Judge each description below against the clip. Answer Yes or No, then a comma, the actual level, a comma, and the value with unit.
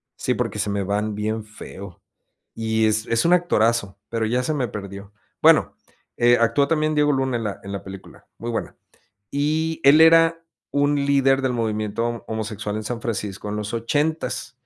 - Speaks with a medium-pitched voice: No, low, 115 Hz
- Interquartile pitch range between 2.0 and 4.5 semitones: No, average, 5.1 semitones